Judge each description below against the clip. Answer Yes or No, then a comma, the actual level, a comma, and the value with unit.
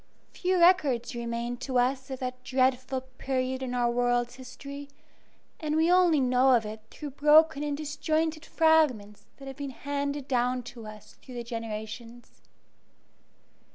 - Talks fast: No, average, 150 wpm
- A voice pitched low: No, very high, 260 Hz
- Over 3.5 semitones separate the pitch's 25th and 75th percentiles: No, average, 3.1 semitones